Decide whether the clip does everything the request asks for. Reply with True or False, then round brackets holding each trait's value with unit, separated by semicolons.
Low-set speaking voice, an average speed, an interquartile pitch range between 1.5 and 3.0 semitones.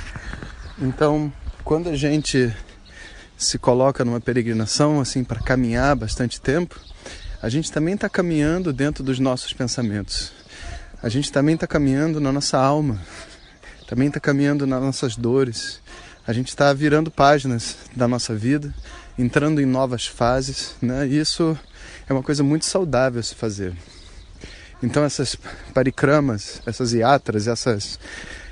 False (130 Hz; 135 wpm; 3.8 semitones)